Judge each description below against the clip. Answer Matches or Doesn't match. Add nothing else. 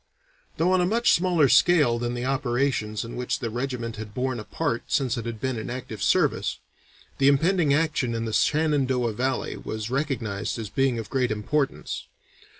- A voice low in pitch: Matches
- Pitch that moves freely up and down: Doesn't match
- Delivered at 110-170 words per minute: Doesn't match